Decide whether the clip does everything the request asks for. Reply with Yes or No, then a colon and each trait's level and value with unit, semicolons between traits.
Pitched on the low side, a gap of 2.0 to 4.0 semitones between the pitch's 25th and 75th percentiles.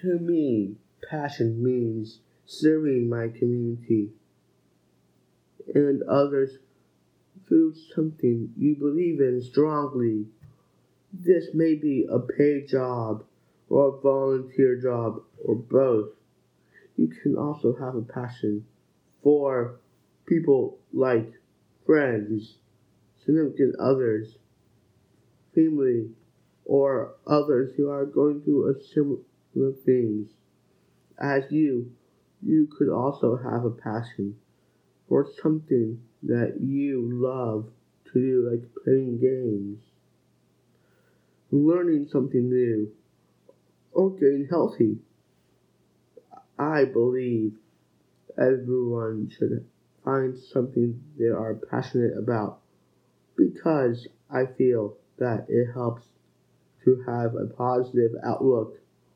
Yes: low, 125 Hz; average, 3.7 semitones